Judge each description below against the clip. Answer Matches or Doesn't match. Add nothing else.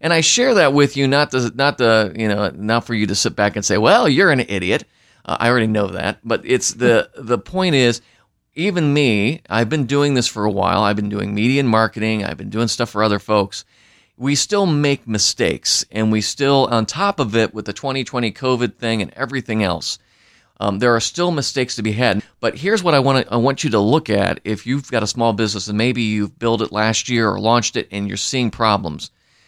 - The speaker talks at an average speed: Doesn't match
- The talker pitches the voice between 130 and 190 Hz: Doesn't match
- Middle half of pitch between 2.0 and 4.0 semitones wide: Doesn't match